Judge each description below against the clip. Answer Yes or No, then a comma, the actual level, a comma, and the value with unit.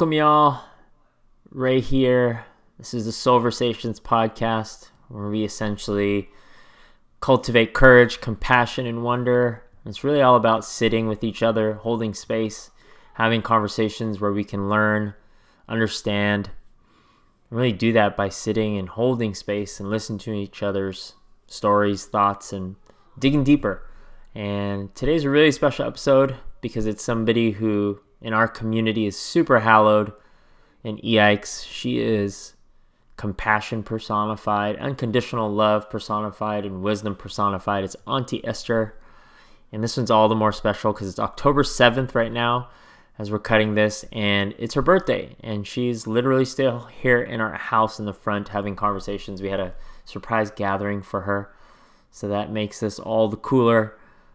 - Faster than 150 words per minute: No, average, 145 wpm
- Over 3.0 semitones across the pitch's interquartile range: No, average, 2.7 semitones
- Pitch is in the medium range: No, low, 110 Hz